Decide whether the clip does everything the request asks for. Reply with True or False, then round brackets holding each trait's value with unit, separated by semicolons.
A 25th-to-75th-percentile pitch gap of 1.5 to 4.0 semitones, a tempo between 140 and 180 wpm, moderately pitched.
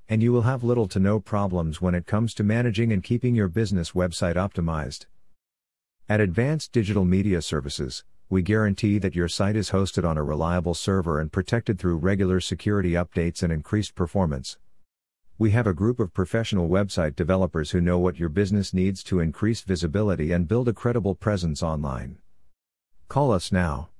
False (3.7 semitones; 175 wpm; 95 Hz)